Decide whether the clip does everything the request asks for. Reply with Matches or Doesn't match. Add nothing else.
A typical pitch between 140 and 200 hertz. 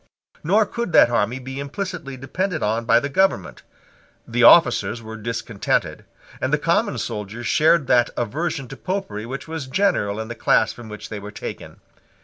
Doesn't match